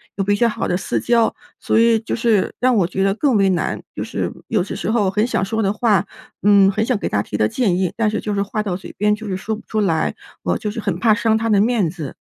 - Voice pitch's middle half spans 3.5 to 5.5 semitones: No, narrow, 2.6 semitones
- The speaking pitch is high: Yes, high, 210 Hz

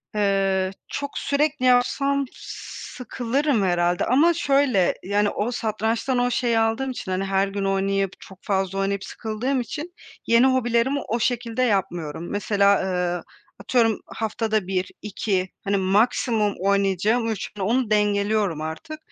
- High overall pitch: Yes, high, 215 Hz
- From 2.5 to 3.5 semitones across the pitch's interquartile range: No, average, 4.1 semitones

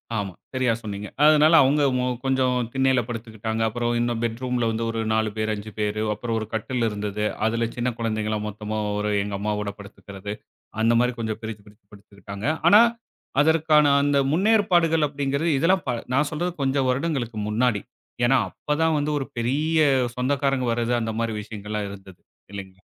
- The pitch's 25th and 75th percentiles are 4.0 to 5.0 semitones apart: Yes, average, 4.7 semitones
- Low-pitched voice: Yes, low, 120 Hz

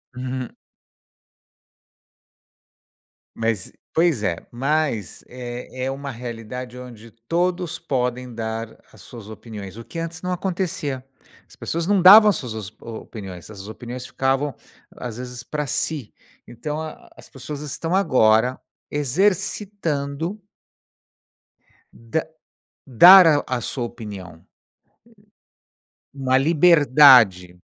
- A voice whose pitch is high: No, low, 130 Hz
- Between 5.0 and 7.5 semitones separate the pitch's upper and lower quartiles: Yes, wide, 5.5 semitones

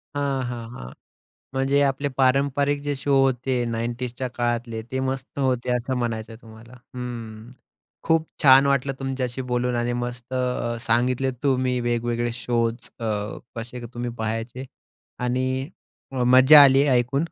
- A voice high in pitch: No, low, 125 Hz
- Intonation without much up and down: Yes, narrow, 2.0 semitones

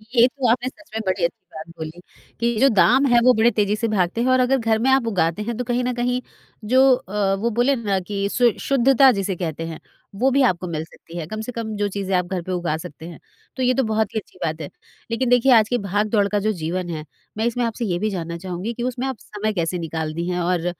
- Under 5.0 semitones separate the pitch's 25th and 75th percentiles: No, average, 5.3 semitones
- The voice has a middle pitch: No, high, 210 Hz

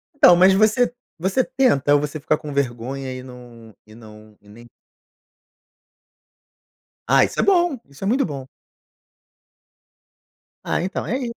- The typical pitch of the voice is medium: Yes, medium, 145 Hz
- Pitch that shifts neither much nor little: No, wide, 8.6 semitones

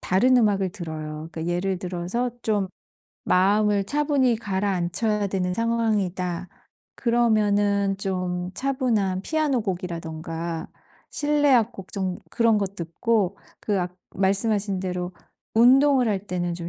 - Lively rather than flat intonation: No, average, 4.1 semitones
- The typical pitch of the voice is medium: No, high, 195 Hz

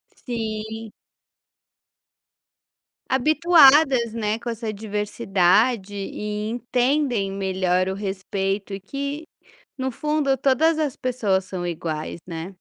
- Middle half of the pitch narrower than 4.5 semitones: No, average, 5.2 semitones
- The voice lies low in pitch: No, high, 220 Hz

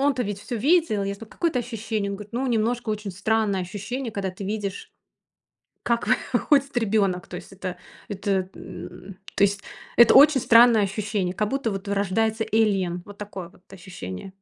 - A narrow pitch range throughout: No, average, 3.2 semitones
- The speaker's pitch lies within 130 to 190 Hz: No, high, 210 Hz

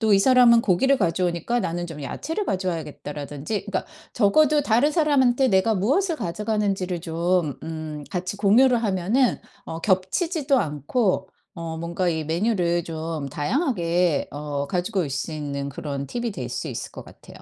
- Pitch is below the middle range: No, medium, 185 Hz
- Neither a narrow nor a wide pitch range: No, wide, 6.4 semitones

